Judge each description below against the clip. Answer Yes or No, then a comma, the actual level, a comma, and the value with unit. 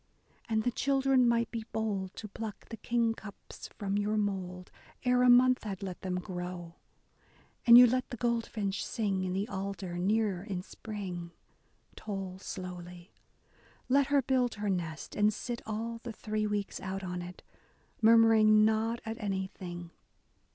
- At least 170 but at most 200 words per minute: No, average, 150 wpm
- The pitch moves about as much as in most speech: Yes, average, 3.6 semitones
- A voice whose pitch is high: Yes, high, 210 Hz